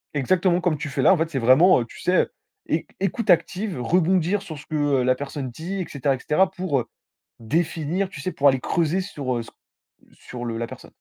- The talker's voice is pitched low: No, medium, 155 Hz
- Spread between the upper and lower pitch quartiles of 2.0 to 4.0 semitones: No, wide, 5.5 semitones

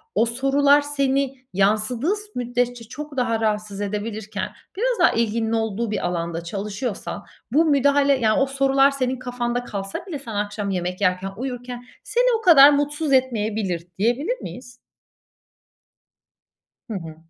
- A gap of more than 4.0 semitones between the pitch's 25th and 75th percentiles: Yes, average, 4.8 semitones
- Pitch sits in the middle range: No, high, 245 Hz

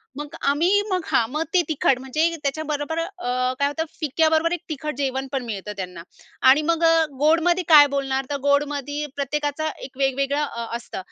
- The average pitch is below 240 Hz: No, very high, 290 Hz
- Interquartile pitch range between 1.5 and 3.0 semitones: Yes, average, 2.7 semitones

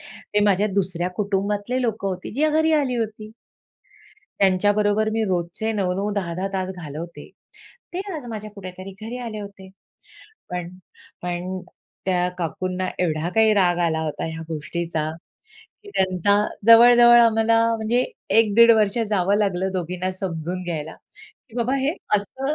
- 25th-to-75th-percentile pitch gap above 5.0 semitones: No, average, 3.8 semitones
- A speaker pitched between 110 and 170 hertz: No, high, 200 Hz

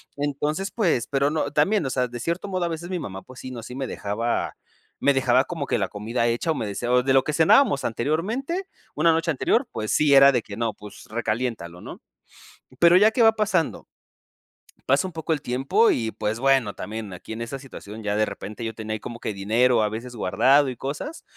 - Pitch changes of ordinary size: No, wide, 6.2 semitones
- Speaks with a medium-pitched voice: No, low, 130 Hz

